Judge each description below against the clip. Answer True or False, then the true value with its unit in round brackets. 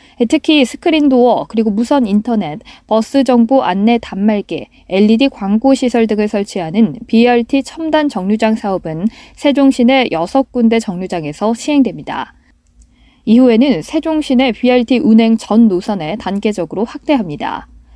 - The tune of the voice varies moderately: True (4.2 semitones)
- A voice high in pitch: True (230 Hz)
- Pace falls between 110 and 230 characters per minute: False (305 characters per minute)